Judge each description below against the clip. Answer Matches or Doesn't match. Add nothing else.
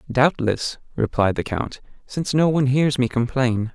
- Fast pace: Doesn't match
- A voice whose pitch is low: Matches